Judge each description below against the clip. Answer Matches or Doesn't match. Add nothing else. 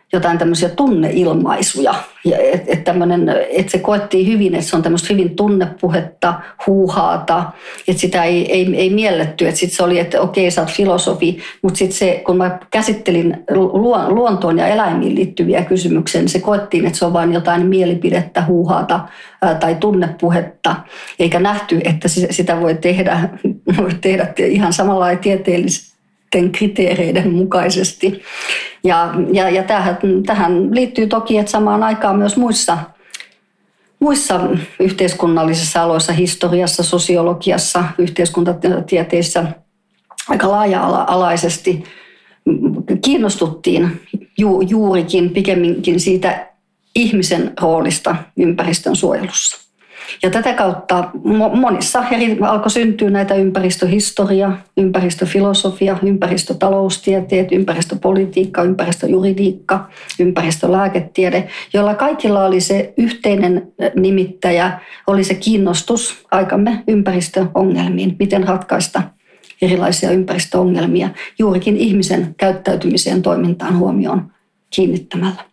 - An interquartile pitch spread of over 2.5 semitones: Doesn't match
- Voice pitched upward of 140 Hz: Matches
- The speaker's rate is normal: Matches